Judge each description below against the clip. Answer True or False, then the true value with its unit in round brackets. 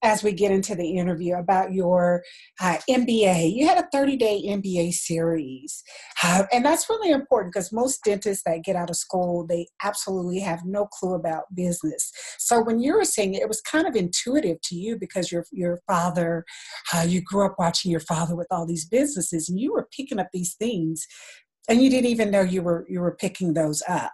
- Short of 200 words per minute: False (205 wpm)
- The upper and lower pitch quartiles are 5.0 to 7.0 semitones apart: False (4.0 semitones)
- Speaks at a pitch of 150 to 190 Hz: True (185 Hz)